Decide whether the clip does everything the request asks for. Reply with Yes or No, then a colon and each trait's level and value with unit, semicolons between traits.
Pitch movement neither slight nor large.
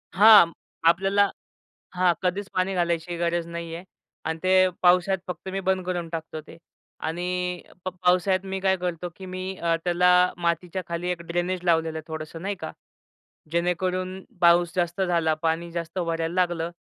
No: narrow, 1.6 semitones